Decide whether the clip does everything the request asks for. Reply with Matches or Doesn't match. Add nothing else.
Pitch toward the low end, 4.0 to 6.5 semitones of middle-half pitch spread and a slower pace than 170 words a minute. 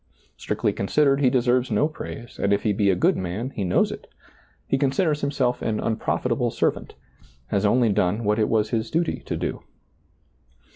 Doesn't match